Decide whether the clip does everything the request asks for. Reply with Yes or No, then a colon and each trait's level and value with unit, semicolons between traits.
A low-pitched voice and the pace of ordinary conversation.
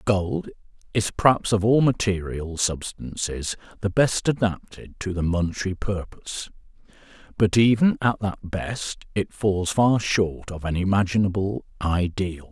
No: low, 100 Hz; slow, 130 wpm